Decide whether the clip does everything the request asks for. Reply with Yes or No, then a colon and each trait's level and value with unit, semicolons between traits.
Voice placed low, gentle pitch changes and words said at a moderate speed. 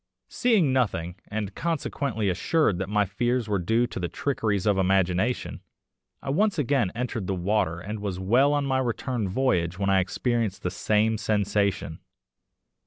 No: low, 105 Hz; average, 4.8 semitones; average, 160 wpm